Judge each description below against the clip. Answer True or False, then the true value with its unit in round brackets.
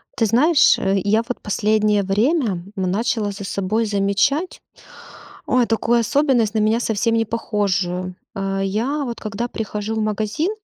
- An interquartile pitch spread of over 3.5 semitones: False (2.8 semitones)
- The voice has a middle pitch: False (215 Hz)